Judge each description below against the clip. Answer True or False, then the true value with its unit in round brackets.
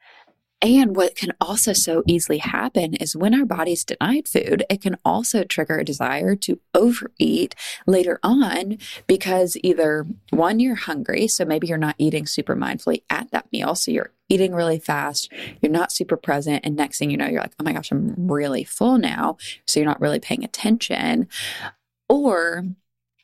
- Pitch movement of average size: False (6.2 semitones)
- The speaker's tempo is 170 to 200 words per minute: True (175 wpm)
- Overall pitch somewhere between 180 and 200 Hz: True (185 Hz)